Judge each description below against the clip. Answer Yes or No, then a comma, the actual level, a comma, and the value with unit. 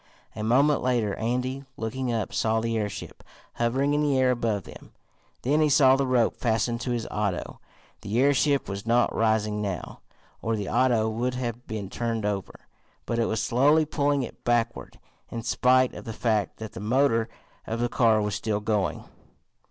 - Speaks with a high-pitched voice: No, low, 115 Hz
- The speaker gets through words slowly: No, average, 180 wpm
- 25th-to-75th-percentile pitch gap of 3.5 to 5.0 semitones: No, average, 2.8 semitones